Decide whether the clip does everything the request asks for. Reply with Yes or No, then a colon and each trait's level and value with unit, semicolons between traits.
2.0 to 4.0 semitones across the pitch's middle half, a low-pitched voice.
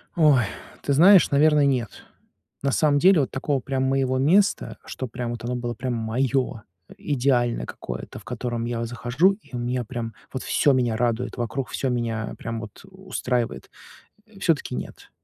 Yes: average, 3.0 semitones; low, 125 Hz